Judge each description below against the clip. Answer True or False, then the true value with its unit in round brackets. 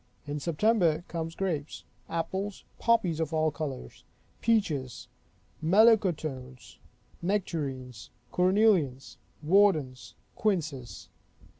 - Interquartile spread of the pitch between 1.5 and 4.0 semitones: False (5.6 semitones)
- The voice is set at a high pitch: False (160 Hz)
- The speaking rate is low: True (80 wpm)